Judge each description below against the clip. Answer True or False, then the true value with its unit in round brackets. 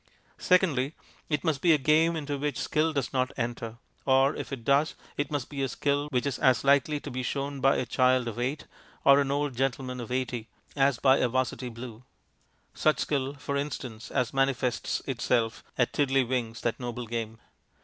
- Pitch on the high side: False (135 Hz)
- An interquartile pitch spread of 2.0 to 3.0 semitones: True (2.6 semitones)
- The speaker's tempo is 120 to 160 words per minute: False (190 wpm)